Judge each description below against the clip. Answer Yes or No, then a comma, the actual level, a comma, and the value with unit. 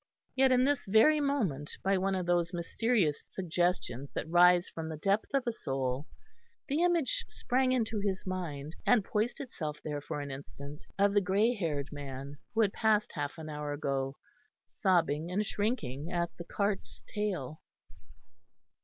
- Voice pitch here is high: No, medium, 180 Hz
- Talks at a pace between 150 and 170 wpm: Yes, average, 160 wpm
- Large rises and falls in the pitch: Yes, wide, 6.6 semitones